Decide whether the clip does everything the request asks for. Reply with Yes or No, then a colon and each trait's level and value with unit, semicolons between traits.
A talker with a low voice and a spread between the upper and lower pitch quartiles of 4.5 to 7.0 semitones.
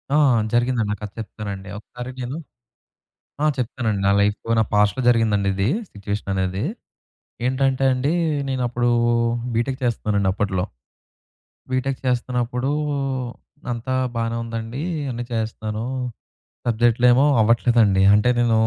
No: low, 115 Hz; average, 3.0 semitones